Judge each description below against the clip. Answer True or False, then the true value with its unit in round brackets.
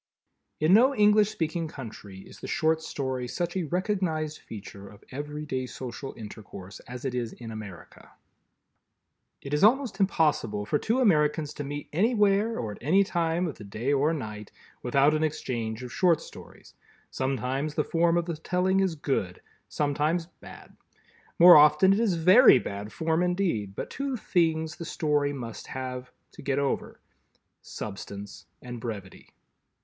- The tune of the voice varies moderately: False (6.0 semitones)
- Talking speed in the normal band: True (155 wpm)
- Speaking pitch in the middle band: True (150 Hz)